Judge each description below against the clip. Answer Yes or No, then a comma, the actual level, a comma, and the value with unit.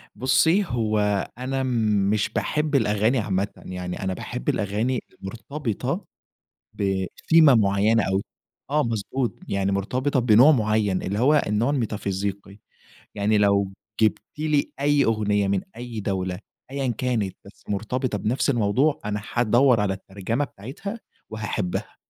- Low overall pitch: Yes, low, 110 Hz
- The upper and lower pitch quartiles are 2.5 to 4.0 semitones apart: No, average, 4.6 semitones